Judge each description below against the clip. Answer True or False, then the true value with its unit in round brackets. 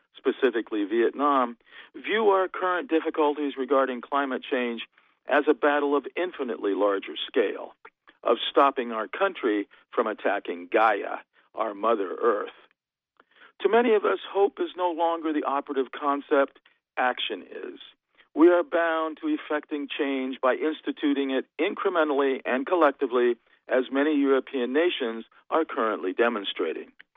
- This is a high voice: False (150 Hz)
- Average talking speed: False (130 wpm)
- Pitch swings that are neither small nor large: False (5.7 semitones)